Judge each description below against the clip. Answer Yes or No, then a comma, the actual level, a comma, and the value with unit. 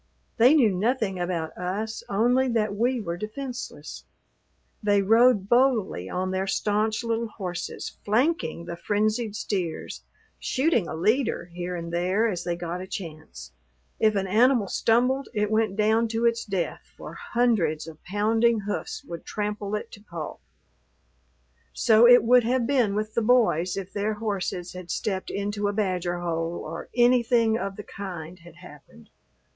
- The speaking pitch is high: Yes, high, 210 Hz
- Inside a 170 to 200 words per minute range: No, average, 155 wpm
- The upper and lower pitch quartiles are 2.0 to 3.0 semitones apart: No, average, 4.3 semitones